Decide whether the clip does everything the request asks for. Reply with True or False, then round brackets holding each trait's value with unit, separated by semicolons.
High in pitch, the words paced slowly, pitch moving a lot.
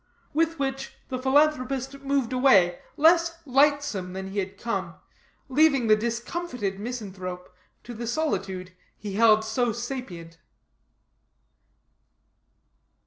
True (240 Hz; 105 wpm; 6.0 semitones)